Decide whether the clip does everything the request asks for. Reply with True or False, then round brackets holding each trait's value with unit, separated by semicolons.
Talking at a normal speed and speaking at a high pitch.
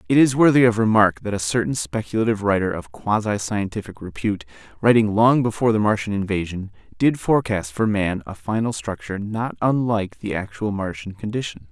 False (170 wpm; 105 Hz)